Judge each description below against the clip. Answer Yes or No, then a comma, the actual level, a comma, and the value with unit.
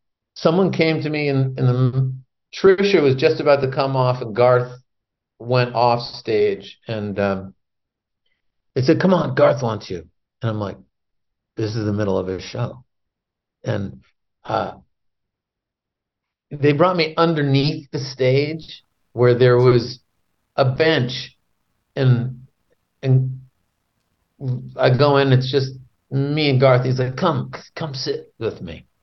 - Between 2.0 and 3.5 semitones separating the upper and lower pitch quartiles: No, average, 4.0 semitones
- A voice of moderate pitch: No, low, 130 Hz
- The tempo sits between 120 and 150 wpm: Yes, average, 140 wpm